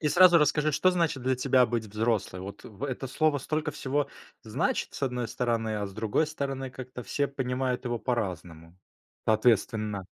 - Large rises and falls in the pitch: No, average, 4.4 semitones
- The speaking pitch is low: Yes, low, 125 Hz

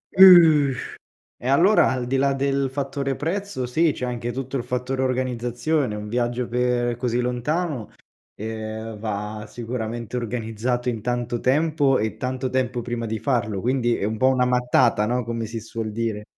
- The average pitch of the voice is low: Yes, low, 125 Hz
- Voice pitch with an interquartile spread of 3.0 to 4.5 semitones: No, narrow, 2.6 semitones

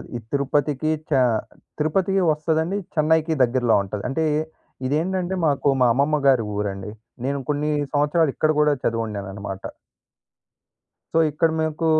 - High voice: No, medium, 150 Hz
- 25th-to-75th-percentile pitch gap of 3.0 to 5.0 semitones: Yes, average, 4.4 semitones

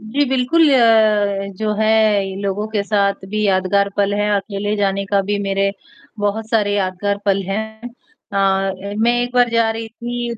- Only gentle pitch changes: Yes, narrow, 2.0 semitones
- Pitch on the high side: Yes, high, 205 Hz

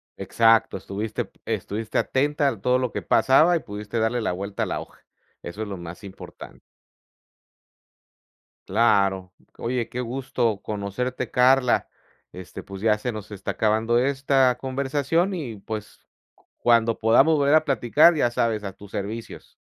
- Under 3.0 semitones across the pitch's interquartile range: No, average, 4.2 semitones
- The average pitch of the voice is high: No, low, 115 Hz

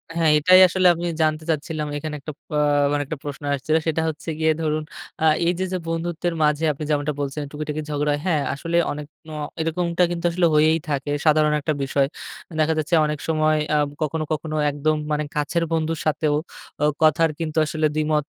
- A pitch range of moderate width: No, narrow, 1.5 semitones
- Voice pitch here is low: No, medium, 155 Hz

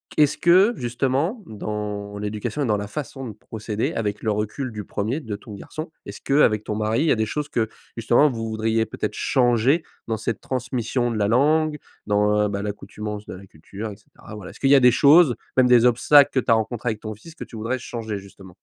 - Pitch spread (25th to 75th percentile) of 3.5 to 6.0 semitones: Yes, average, 4.0 semitones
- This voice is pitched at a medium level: No, low, 115 Hz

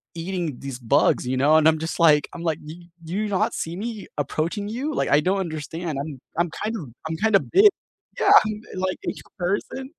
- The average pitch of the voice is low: No, medium, 170 Hz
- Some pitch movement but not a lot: Yes, average, 5.0 semitones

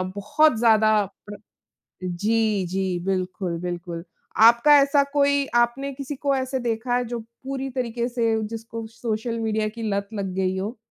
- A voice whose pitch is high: Yes, high, 225 Hz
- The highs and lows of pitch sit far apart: No, average, 3.7 semitones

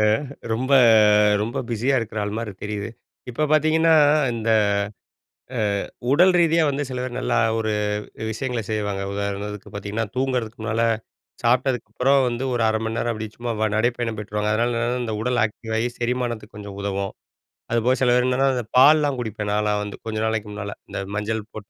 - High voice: No, low, 115 Hz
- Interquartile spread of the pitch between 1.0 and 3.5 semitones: Yes, average, 3.0 semitones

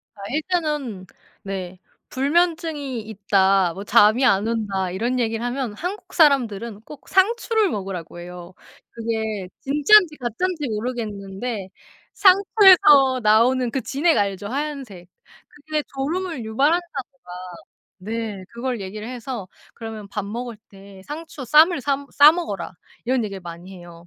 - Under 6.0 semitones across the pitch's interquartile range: No, wide, 6.6 semitones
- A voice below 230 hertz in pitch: No, high, 235 Hz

